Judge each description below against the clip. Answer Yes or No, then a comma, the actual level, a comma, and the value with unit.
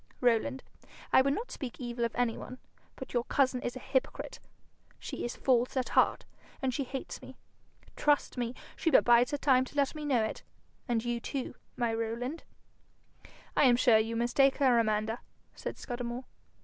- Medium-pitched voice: No, high, 245 Hz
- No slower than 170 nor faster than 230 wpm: Yes, average, 180 wpm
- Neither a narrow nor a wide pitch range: No, narrow, 2.2 semitones